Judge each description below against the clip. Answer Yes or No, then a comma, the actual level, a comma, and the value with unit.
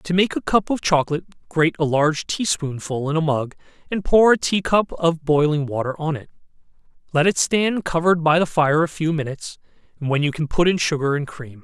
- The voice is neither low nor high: Yes, medium, 160 Hz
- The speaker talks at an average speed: No, fast, 215 wpm